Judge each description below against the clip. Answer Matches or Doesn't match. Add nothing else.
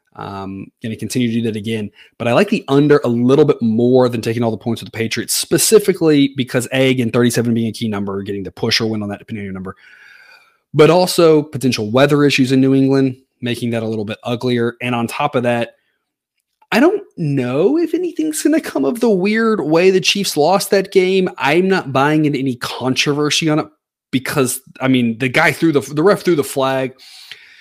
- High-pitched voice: Doesn't match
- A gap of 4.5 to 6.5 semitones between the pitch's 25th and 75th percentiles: Matches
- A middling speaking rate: Doesn't match